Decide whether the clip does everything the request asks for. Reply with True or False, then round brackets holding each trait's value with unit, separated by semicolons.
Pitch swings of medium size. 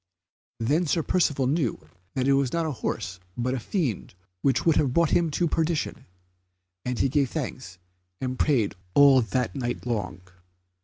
True (4.1 semitones)